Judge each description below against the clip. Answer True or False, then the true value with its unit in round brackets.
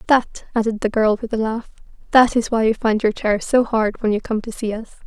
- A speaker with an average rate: False (250 wpm)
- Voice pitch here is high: True (225 Hz)